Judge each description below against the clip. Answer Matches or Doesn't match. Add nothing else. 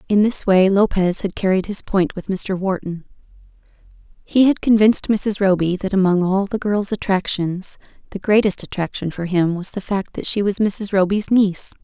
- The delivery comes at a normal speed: Matches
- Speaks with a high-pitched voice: Matches